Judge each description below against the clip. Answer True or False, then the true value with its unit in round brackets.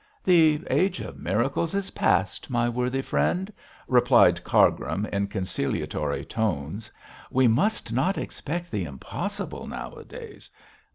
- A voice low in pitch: True (120 Hz)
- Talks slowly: True (115 wpm)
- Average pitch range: False (9.0 semitones)